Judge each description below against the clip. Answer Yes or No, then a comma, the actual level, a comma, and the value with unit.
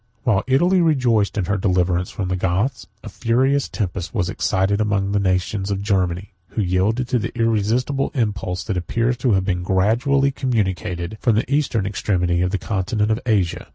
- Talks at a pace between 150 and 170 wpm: No, average, 180 wpm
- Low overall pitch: Yes, low, 100 Hz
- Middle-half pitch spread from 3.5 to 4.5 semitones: Yes, average, 4.1 semitones